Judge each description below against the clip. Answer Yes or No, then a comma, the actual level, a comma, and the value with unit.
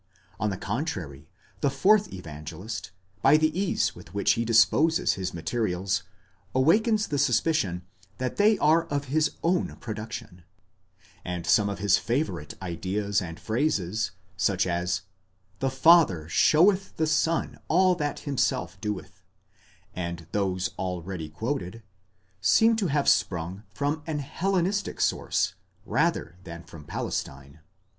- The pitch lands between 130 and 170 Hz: No, low, 110 Hz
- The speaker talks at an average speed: No, slow, 130 wpm